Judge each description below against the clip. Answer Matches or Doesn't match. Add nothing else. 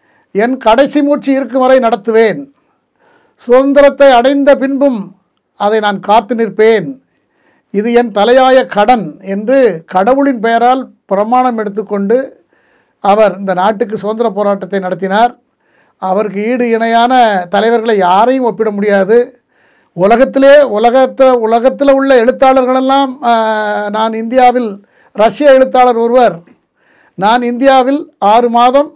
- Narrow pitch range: Doesn't match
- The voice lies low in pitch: Doesn't match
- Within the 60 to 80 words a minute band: Doesn't match